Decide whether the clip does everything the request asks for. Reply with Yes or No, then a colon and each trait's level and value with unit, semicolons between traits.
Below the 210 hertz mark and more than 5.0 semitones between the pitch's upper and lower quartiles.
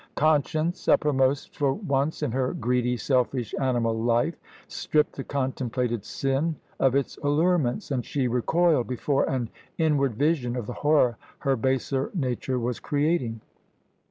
No: low, 135 Hz; average, 3.2 semitones